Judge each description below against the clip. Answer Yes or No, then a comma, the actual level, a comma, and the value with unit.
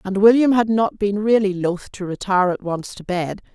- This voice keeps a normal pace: No, fast, 220 wpm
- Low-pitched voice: No, high, 200 Hz